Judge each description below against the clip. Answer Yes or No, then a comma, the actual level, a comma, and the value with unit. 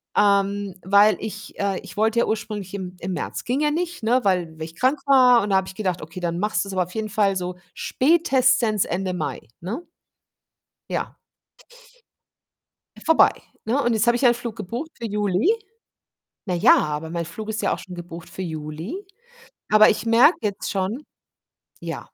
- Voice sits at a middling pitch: No, high, 205 Hz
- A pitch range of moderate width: Yes, average, 4.5 semitones